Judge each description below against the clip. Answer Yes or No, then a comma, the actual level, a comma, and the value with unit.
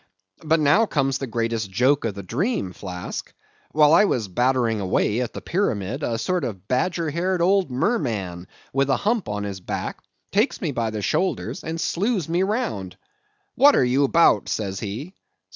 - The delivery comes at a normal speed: Yes, average, 175 wpm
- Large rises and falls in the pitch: Yes, wide, 8.6 semitones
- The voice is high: No, low, 135 Hz